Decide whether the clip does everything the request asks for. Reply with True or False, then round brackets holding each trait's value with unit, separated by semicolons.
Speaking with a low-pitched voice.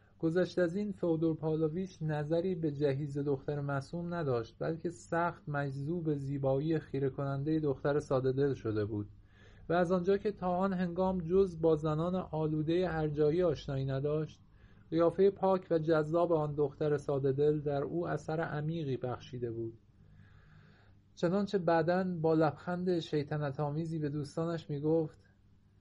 False (155 Hz)